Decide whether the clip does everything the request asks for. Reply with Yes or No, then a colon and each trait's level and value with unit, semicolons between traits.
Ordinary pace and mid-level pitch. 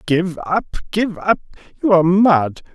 Yes: average, 155 wpm; medium, 180 Hz